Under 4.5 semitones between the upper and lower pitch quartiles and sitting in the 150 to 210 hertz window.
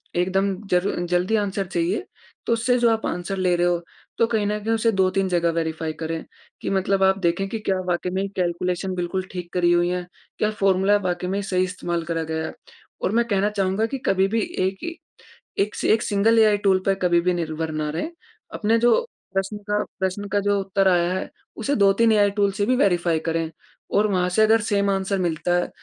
Yes: average, 2.8 semitones; high, 190 Hz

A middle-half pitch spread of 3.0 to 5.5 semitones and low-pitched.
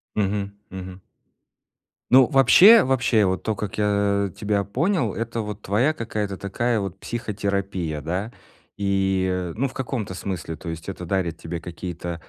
Yes: average, 3.6 semitones; low, 100 Hz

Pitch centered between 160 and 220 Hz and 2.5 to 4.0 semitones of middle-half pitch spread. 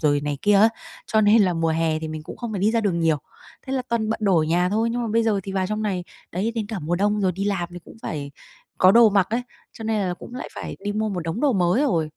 No: high, 200 Hz; average, 4.4 semitones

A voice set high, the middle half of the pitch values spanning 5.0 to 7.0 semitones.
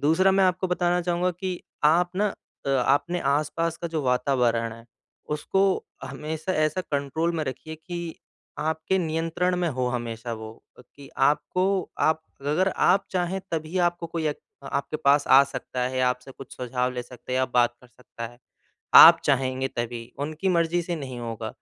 No: medium, 150 Hz; average, 5.3 semitones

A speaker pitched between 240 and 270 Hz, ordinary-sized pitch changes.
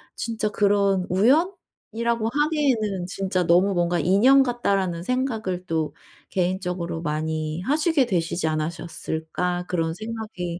No: high, 190 Hz; average, 5.0 semitones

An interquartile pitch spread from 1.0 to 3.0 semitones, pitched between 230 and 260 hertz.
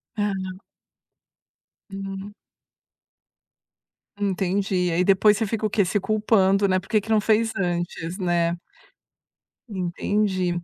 No: narrow, 2.5 semitones; high, 195 Hz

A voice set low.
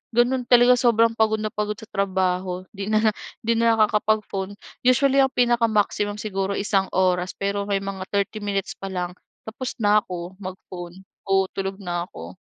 No: high, 205 Hz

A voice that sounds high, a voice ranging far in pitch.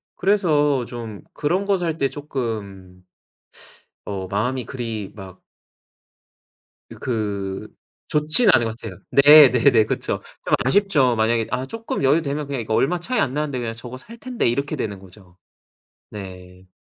No: low, 125 Hz; wide, 6.1 semitones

